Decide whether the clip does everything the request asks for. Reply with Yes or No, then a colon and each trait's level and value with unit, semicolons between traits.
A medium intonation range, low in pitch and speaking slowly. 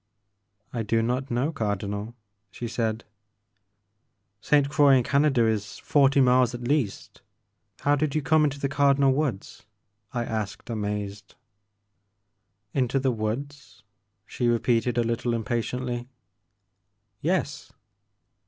Yes: average, 4.0 semitones; low, 120 Hz; slow, 130 wpm